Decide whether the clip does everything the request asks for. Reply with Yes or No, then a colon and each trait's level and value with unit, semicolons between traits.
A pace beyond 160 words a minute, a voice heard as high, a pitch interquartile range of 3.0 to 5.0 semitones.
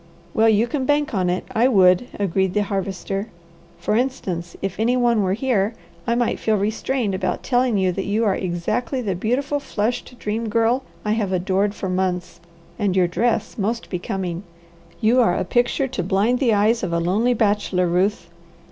Yes: average, 185 wpm; high, 210 Hz; average, 4.1 semitones